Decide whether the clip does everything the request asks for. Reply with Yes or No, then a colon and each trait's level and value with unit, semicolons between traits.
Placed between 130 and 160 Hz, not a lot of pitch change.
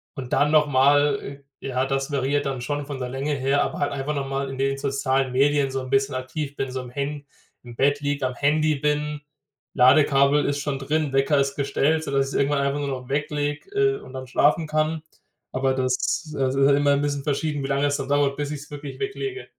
Yes: medium, 140 Hz; narrow, 1.3 semitones